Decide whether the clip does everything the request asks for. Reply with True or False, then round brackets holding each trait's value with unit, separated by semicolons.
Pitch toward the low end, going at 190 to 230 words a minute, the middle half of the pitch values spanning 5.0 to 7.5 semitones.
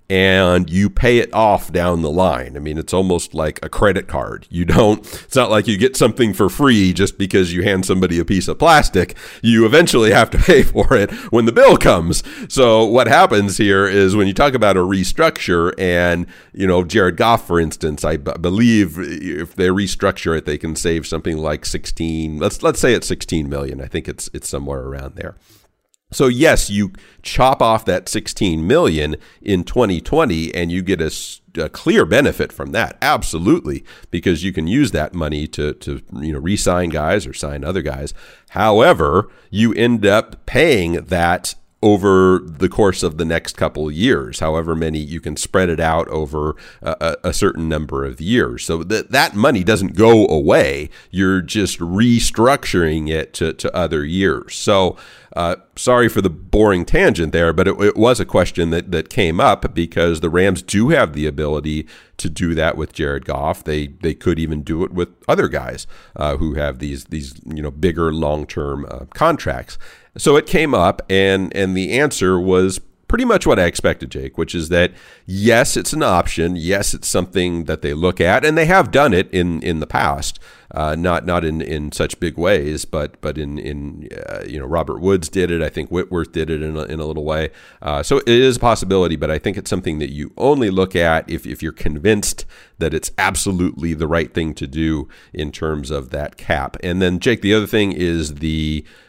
False (85 Hz; 200 wpm; 3.6 semitones)